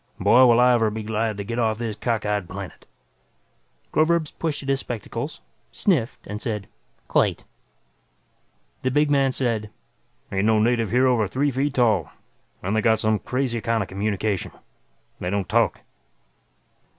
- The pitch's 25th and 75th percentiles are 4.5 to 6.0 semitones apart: No, average, 3.5 semitones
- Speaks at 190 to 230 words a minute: No, average, 155 wpm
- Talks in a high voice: No, low, 115 Hz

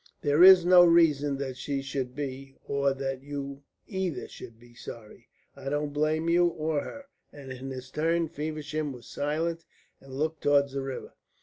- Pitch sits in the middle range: Yes, medium, 145 Hz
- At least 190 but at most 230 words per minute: No, average, 175 wpm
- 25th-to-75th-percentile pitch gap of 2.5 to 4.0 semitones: Yes, average, 2.8 semitones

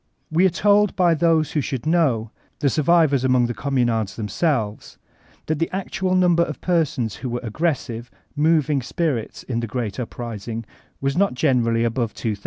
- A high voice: No, low, 135 Hz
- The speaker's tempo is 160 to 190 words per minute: Yes, average, 170 wpm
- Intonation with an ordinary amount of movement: No, wide, 6.0 semitones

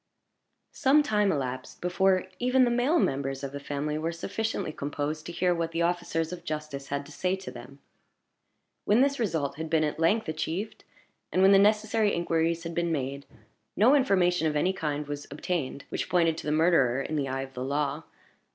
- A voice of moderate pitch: Yes, medium, 165 Hz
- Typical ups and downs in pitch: Yes, average, 4.8 semitones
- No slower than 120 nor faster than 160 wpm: No, average, 195 wpm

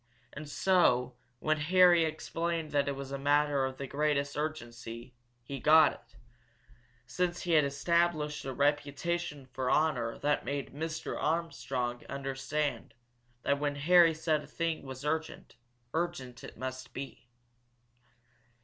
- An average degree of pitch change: Yes, average, 3.1 semitones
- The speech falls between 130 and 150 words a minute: Yes, slow, 135 wpm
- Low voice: No, medium, 145 Hz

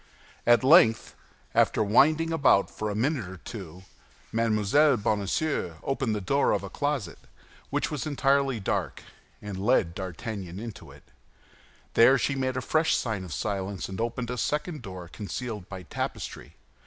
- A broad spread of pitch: Yes, wide, 5.8 semitones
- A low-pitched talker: Yes, low, 115 Hz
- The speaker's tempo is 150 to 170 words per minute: Yes, average, 155 wpm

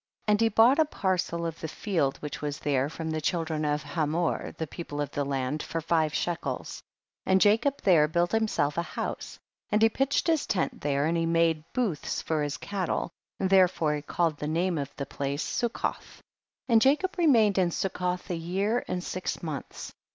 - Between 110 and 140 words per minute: No, fast, 205 wpm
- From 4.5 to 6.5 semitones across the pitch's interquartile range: Yes, average, 5.0 semitones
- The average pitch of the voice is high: No, medium, 170 Hz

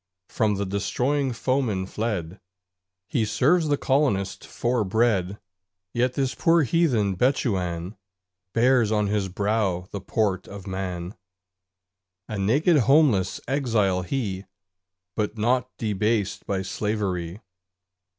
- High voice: No, low, 105 Hz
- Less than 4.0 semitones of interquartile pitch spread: No, average, 4.8 semitones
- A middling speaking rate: No, slow, 110 wpm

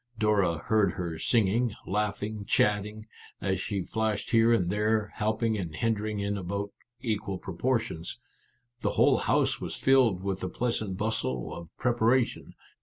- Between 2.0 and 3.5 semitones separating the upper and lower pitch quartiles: Yes, narrow, 2.6 semitones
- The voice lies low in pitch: Yes, low, 105 Hz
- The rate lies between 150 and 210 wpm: No, average, 140 wpm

